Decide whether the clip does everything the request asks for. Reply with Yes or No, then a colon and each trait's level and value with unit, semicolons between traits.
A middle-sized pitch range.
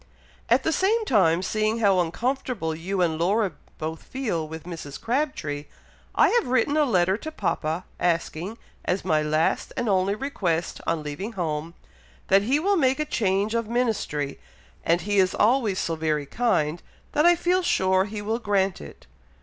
No: wide, 6.5 semitones